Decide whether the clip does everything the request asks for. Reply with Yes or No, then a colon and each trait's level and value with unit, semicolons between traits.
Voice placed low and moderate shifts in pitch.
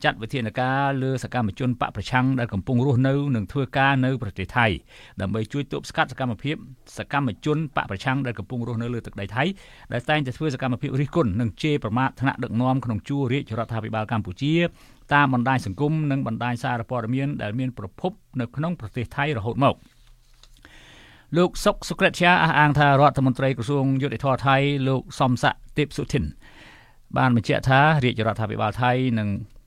Yes: low, 130 Hz; average, 3.2 semitones